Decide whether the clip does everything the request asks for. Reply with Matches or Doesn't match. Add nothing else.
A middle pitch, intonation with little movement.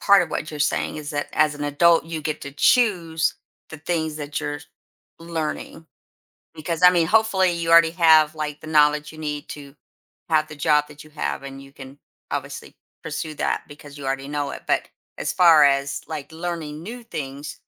Matches